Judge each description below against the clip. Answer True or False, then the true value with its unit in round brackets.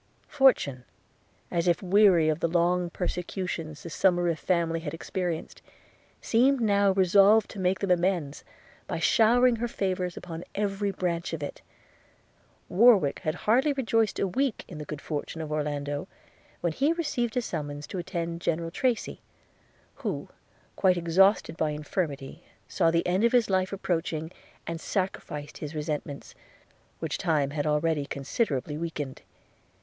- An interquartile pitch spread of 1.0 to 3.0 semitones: False (4.2 semitones)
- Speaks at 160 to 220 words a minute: False (145 wpm)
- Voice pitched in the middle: True (175 Hz)